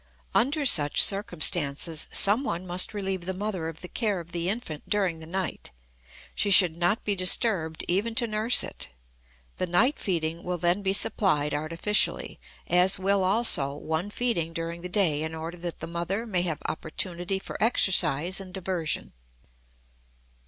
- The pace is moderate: Yes, average, 160 wpm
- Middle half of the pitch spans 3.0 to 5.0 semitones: Yes, average, 3.4 semitones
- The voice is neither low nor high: Yes, medium, 180 Hz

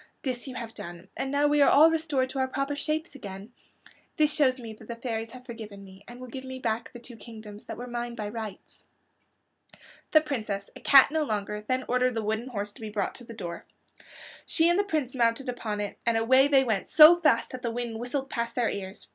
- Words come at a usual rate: No, fast, 230 wpm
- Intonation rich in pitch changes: No, average, 3.6 semitones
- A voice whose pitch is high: Yes, high, 240 Hz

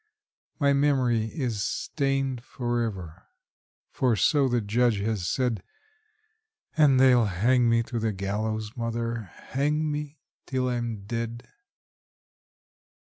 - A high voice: No, low, 120 Hz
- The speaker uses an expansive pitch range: No, average, 3.3 semitones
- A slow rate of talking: Yes, slow, 110 wpm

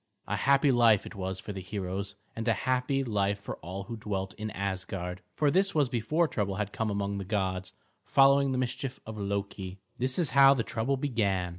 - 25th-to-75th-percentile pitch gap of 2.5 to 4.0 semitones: No, average, 4.9 semitones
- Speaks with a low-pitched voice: Yes, low, 105 Hz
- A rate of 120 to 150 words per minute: No, average, 200 wpm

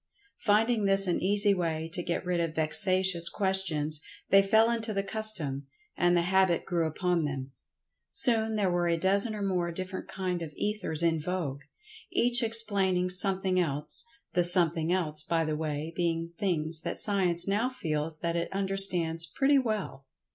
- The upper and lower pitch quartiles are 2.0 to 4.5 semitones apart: Yes, average, 3.3 semitones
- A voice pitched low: No, medium, 180 Hz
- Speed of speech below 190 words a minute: Yes, average, 160 wpm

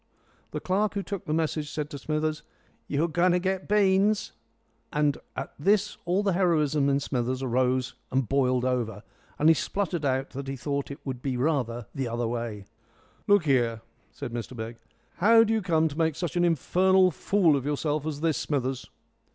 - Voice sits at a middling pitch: Yes, medium, 150 Hz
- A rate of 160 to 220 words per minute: Yes, average, 185 wpm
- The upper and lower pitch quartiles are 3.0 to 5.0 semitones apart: No, wide, 5.6 semitones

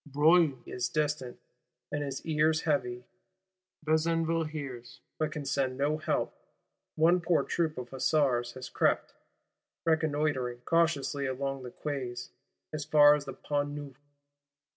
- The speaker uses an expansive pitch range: No, average, 2.9 semitones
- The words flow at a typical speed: No, slow, 130 wpm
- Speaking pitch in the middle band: Yes, medium, 145 Hz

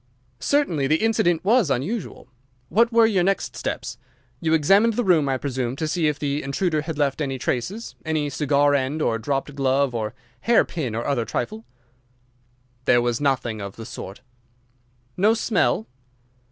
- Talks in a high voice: No, medium, 145 Hz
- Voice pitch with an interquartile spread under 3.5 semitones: No, wide, 5.6 semitones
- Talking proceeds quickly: No, average, 155 wpm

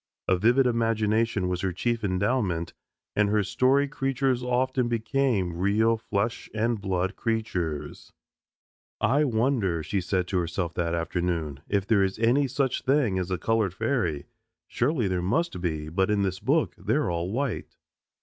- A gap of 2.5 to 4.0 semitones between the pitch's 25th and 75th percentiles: No, average, 5.3 semitones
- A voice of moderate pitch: No, low, 105 Hz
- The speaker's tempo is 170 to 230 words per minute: No, average, 155 wpm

